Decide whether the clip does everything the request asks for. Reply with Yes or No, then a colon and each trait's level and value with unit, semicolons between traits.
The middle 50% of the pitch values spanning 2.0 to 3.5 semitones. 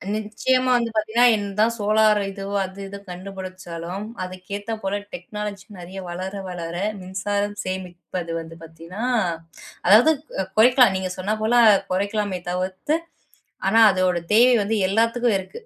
Yes: average, 2.9 semitones